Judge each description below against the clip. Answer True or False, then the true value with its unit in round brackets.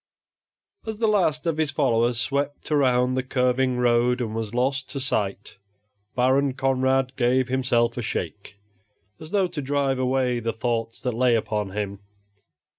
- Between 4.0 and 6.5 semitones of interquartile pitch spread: False (2.6 semitones)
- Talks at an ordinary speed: True (155 wpm)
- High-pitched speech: False (130 Hz)